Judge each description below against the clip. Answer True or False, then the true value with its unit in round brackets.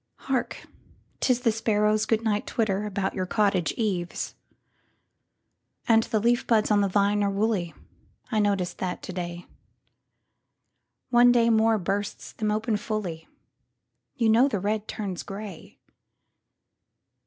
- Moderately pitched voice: False (205 Hz)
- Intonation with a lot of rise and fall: False (3.5 semitones)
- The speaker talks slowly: True (115 wpm)